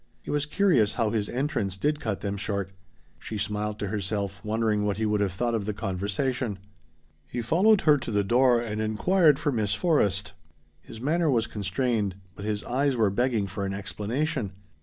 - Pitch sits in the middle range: No, low, 110 Hz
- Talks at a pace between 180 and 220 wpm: Yes, average, 185 wpm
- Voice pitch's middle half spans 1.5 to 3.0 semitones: No, average, 4.2 semitones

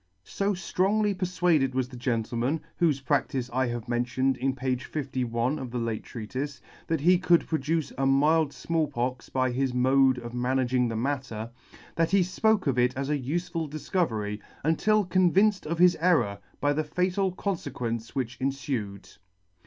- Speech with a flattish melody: No, average, 5.1 semitones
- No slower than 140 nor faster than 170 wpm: Yes, average, 160 wpm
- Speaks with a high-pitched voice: No, low, 135 Hz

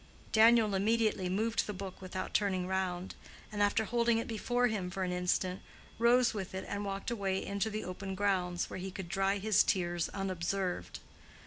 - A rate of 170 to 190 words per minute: Yes, average, 180 wpm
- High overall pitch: Yes, high, 195 Hz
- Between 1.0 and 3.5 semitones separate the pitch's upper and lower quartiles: Yes, average, 2.7 semitones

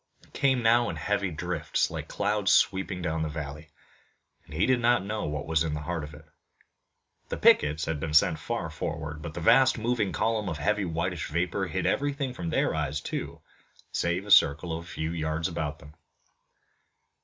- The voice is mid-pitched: No, very low, 85 Hz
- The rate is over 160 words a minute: Yes, average, 190 wpm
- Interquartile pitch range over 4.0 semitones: Yes, average, 5.1 semitones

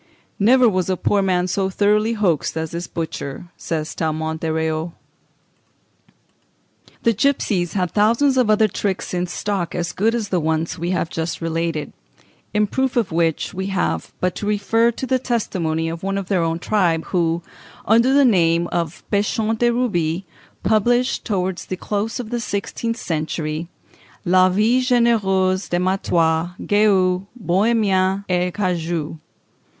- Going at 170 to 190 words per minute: No, average, 155 wpm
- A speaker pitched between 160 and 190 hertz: Yes, medium, 185 Hz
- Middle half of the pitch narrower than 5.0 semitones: Yes, average, 4.3 semitones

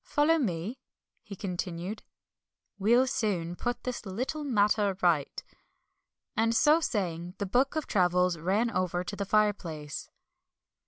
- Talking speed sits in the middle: No, slow, 125 wpm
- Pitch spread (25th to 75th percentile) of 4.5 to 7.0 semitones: Yes, average, 5.1 semitones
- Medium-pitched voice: No, high, 200 Hz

